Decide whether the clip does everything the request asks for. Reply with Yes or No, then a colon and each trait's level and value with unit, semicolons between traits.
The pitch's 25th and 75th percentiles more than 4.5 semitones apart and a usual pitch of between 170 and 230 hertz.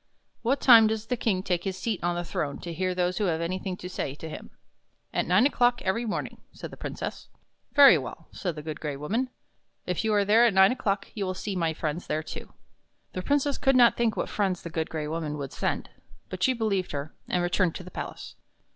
Yes: average, 5.1 semitones; medium, 185 Hz